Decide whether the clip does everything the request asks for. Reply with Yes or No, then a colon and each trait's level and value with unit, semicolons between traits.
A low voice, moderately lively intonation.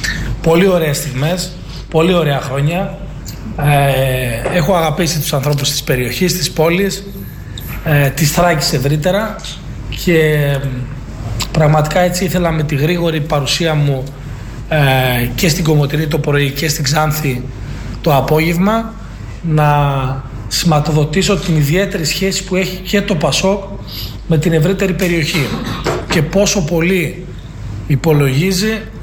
No: medium, 155 Hz; average, 4.1 semitones